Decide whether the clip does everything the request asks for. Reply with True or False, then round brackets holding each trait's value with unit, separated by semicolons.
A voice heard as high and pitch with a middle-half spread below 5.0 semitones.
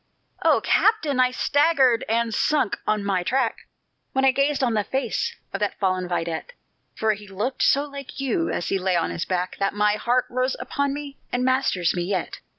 False (235 Hz; 5.6 semitones)